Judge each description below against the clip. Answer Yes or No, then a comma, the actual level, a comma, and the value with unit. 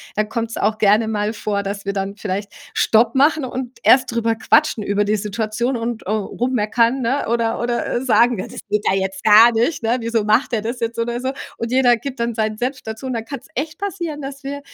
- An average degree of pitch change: Yes, average, 3.0 semitones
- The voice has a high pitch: Yes, high, 230 Hz